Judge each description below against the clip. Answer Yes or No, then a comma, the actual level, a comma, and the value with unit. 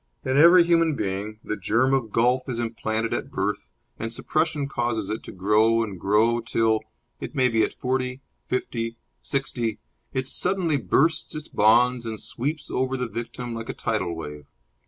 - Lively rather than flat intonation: No, average, 3.2 semitones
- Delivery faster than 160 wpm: Yes, average, 170 wpm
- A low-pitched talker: Yes, low, 120 Hz